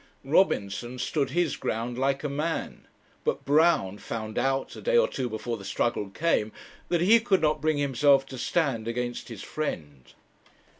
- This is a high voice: No, low, 135 Hz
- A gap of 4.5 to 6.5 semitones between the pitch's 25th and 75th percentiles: Yes, average, 5.1 semitones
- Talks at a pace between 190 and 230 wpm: No, average, 165 wpm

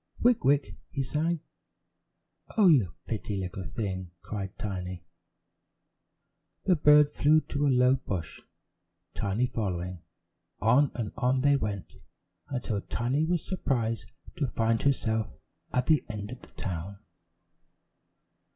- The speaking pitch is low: Yes, low, 120 Hz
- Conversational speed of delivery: No, slow, 125 wpm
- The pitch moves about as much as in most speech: No, wide, 6.2 semitones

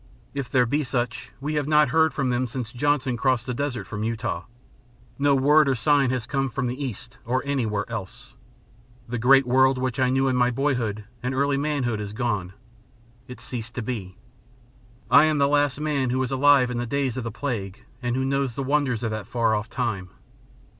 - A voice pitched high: No, low, 130 Hz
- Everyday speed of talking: No, fast, 210 wpm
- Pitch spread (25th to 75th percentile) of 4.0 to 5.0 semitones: No, average, 2.9 semitones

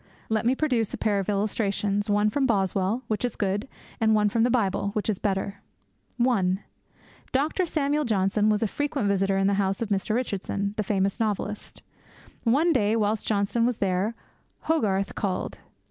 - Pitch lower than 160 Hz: No, high, 210 Hz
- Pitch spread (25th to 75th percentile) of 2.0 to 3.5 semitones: Yes, average, 2.8 semitones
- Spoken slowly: No, average, 175 wpm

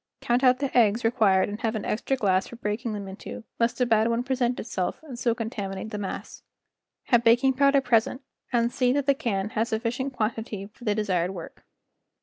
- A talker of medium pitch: No, high, 230 Hz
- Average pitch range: Yes, average, 3.1 semitones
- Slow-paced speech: No, fast, 205 wpm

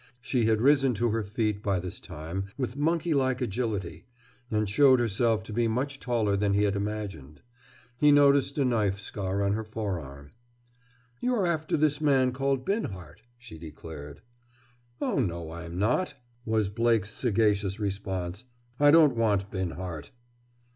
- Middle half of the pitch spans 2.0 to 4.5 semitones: No, average, 5.2 semitones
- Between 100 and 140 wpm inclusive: No, average, 150 wpm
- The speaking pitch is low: Yes, low, 110 Hz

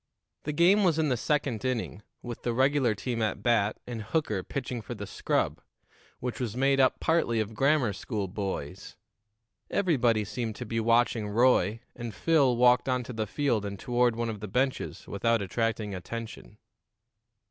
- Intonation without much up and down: No, average, 3.3 semitones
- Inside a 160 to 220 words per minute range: Yes, average, 170 wpm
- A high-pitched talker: No, low, 120 Hz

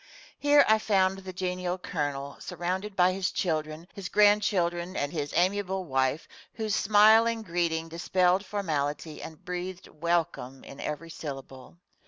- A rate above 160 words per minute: No, slow, 135 wpm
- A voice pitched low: No, medium, 180 Hz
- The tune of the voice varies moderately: Yes, average, 3.6 semitones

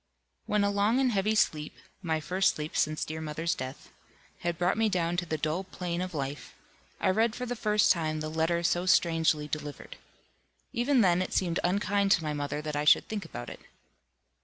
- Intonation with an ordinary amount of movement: Yes, average, 4.5 semitones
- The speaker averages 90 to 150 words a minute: No, average, 200 wpm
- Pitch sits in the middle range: Yes, medium, 170 Hz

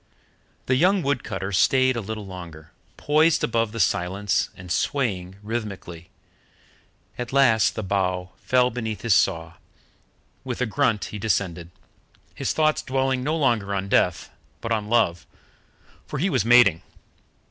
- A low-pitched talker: Yes, low, 110 Hz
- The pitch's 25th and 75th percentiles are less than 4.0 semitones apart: No, average, 5.3 semitones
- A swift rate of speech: No, average, 145 wpm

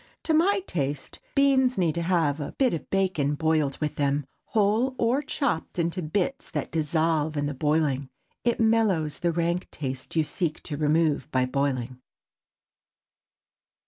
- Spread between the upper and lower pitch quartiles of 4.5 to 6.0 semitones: Yes, wide, 5.6 semitones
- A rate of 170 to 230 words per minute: No, average, 145 wpm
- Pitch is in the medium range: Yes, medium, 160 Hz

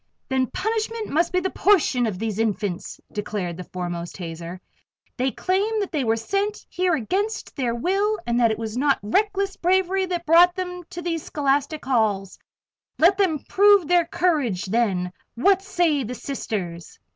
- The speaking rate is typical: Yes, average, 165 wpm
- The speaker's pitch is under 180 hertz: No, very high, 295 Hz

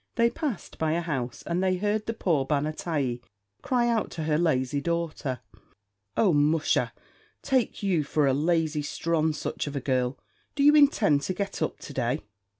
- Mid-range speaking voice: Yes, medium, 160 Hz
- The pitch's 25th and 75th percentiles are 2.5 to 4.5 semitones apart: No, average, 5.2 semitones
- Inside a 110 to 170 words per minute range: No, average, 180 wpm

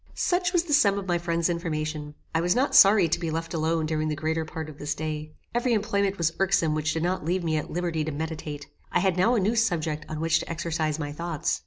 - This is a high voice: No, medium, 165 Hz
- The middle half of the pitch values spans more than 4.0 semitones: No, average, 3.4 semitones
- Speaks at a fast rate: Yes, fast, 245 wpm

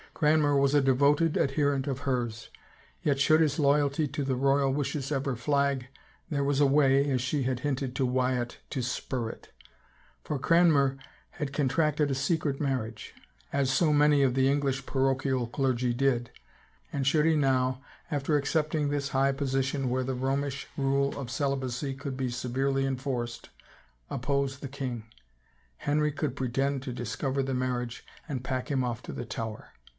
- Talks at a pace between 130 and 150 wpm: No, average, 165 wpm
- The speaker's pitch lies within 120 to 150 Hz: Yes, low, 135 Hz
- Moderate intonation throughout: No, narrow, 1.8 semitones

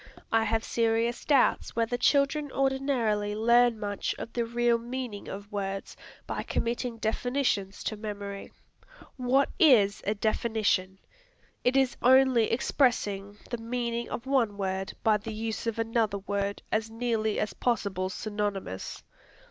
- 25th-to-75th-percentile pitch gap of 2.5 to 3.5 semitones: Yes, average, 3.0 semitones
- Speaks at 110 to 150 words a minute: Yes, slow, 135 wpm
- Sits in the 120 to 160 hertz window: No, high, 225 Hz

